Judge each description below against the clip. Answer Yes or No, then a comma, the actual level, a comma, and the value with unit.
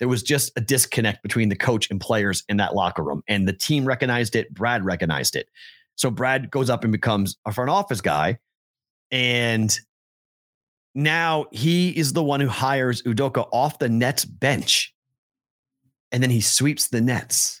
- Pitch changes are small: No, average, 3.7 semitones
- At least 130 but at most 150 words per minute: No, average, 175 wpm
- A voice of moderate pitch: No, low, 125 Hz